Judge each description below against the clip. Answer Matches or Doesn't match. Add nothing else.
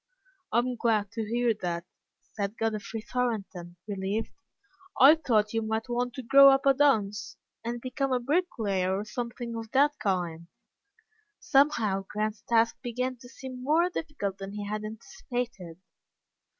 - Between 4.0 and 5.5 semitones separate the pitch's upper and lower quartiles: Doesn't match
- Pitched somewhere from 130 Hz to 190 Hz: Doesn't match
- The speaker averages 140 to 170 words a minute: Matches